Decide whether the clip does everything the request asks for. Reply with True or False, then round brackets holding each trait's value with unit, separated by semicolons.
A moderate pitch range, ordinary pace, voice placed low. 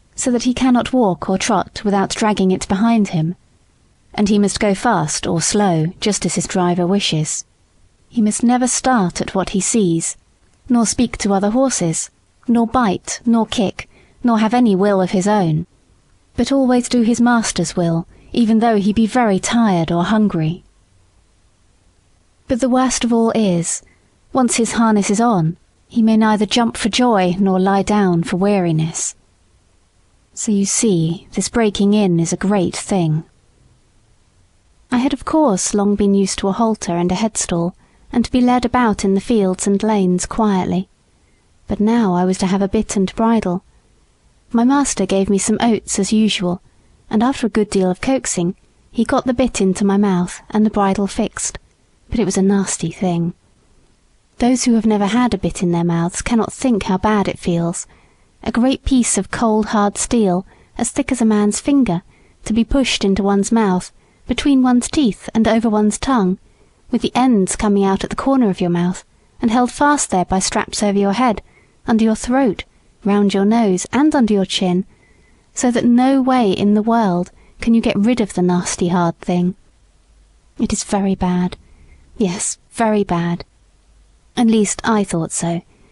False (4.4 semitones; 180 wpm; 205 Hz)